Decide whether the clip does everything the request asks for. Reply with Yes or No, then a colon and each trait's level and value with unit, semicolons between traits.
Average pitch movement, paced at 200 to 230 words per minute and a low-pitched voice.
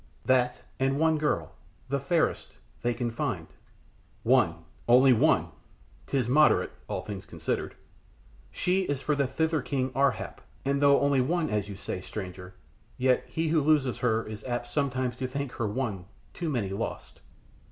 No: average, 3.3 semitones; average, 165 wpm; low, 130 Hz